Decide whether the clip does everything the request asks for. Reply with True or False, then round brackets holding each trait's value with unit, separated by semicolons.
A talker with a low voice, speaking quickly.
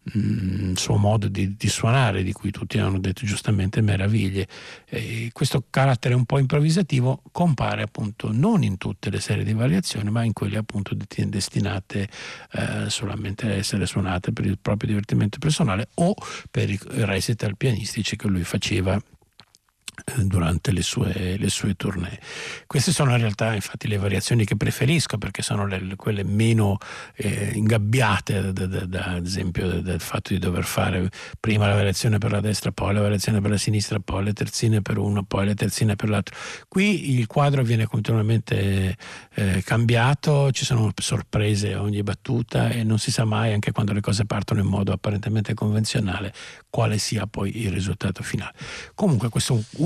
True (105 Hz; 175 wpm)